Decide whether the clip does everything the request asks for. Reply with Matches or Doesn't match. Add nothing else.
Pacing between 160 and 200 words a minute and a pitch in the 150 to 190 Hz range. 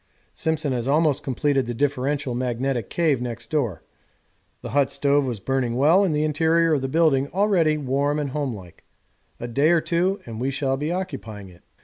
Doesn't match